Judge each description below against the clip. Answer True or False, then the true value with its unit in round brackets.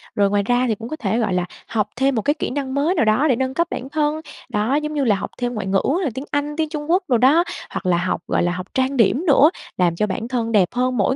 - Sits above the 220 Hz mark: True (250 Hz)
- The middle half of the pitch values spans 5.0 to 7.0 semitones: True (5.5 semitones)